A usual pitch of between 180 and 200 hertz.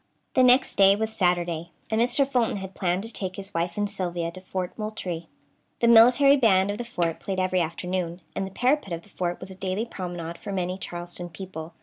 Yes: high, 190 Hz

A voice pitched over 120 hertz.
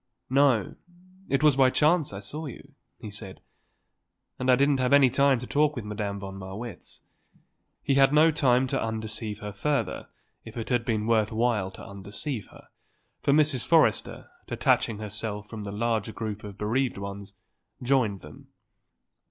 No: low, 115 Hz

